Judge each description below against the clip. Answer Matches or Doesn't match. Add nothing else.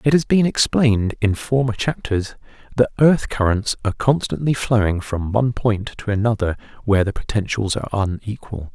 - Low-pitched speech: Matches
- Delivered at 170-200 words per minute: Doesn't match